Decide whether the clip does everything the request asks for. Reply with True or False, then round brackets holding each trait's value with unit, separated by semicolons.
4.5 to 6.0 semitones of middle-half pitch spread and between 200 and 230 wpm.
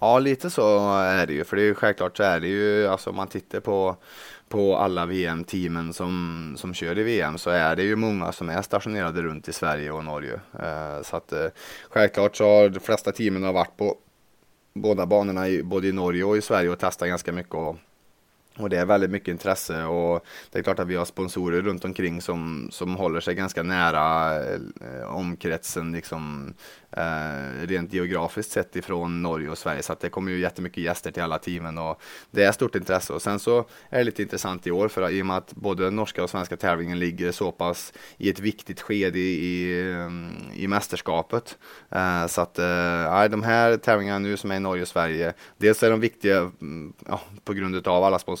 False (2.6 semitones; 205 wpm)